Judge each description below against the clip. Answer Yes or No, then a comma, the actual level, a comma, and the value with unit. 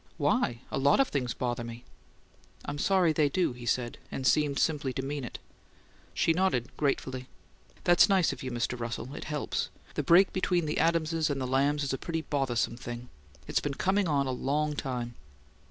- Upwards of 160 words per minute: Yes, average, 190 wpm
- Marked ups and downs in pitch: No, average, 4.2 semitones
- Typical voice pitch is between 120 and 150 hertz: Yes, medium, 140 Hz